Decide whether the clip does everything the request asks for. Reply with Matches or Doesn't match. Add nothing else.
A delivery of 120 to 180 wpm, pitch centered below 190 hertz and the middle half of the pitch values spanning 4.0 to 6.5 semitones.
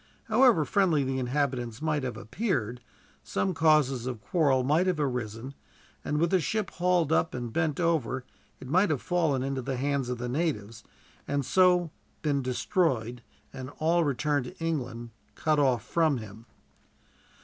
Matches